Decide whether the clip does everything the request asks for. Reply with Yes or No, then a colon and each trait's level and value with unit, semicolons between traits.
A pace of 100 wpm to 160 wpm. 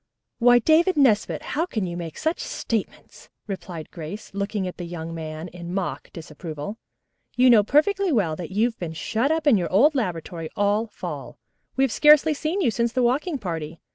No: average, 185 wpm